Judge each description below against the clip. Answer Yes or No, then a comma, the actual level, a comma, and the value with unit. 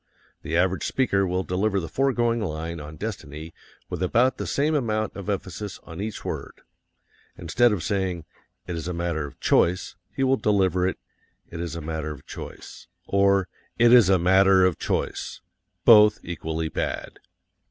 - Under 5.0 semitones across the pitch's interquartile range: Yes, average, 4.2 semitones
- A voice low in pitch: Yes, very low, 95 Hz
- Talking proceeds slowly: No, average, 165 wpm